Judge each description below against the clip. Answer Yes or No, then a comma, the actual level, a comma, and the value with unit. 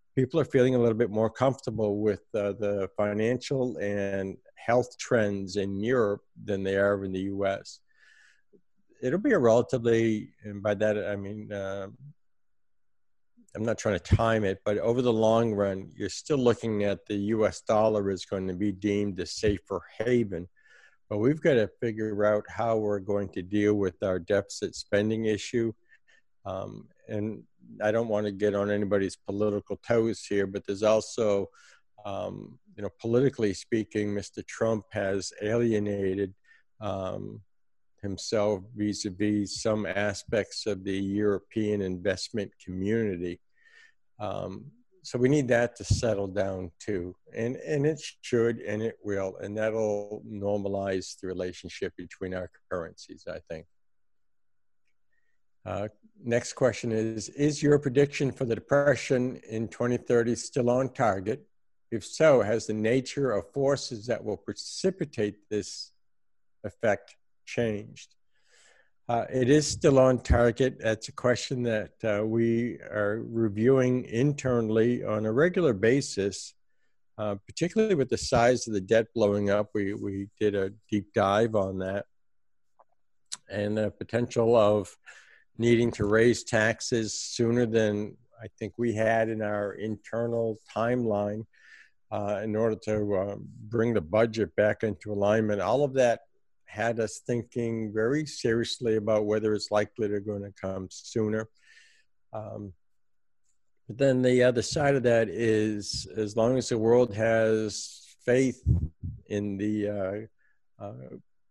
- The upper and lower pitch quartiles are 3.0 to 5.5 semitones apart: No, narrow, 2.6 semitones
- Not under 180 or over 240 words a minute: No, average, 145 wpm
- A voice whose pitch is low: Yes, low, 110 Hz